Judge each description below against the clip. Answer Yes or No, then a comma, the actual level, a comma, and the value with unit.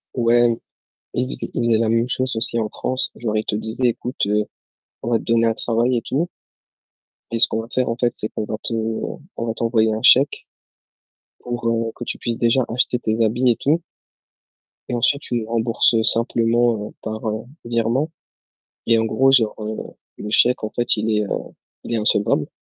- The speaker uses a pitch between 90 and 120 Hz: Yes, low, 115 Hz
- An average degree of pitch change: No, narrow, 1.6 semitones